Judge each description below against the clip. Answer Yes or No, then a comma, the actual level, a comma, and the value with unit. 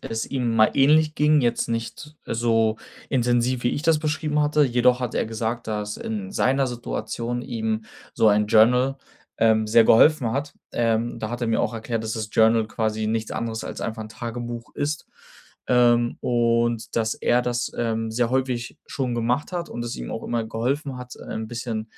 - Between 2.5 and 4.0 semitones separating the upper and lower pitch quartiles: No, narrow, 2.0 semitones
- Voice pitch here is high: No, low, 120 Hz